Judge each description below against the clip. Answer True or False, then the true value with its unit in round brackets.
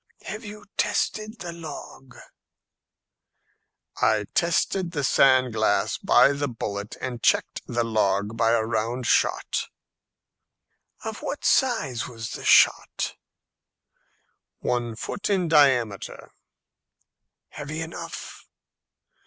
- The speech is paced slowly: True (105 wpm)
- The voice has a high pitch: False (130 Hz)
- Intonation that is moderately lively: False (7.0 semitones)